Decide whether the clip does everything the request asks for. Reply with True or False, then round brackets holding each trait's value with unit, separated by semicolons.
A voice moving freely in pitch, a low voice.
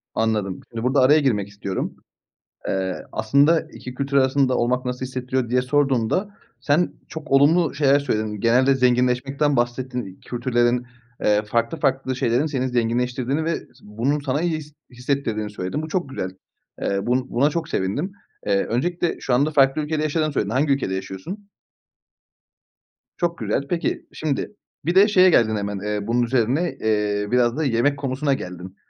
False (4.4 semitones; 130 Hz)